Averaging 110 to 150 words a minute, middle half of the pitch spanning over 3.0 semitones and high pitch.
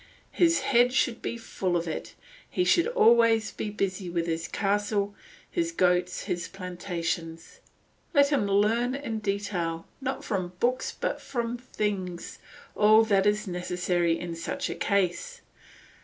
Yes: average, 140 wpm; average, 5.1 semitones; high, 205 Hz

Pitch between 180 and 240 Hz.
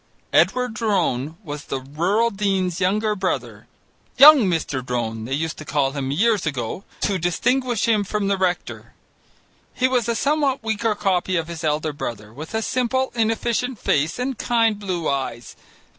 Yes: high, 190 Hz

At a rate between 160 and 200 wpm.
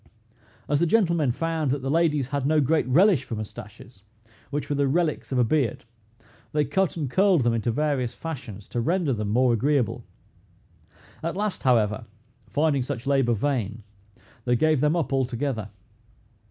Yes: average, 165 wpm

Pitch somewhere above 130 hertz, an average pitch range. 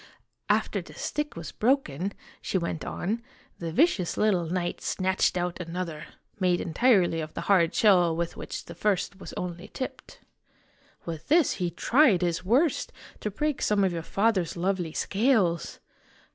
Yes: medium, 185 Hz; average, 3.9 semitones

